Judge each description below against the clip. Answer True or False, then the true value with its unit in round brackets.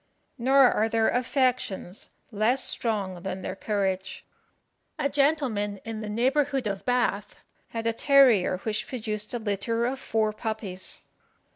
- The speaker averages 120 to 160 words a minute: True (135 wpm)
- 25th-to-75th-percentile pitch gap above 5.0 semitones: False (3.7 semitones)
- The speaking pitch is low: False (225 Hz)